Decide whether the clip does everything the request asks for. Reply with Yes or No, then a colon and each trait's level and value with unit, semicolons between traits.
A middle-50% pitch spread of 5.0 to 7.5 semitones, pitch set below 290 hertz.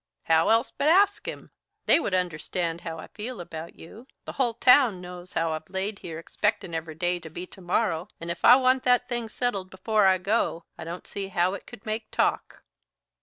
Yes: average, 5.3 semitones; high, 190 Hz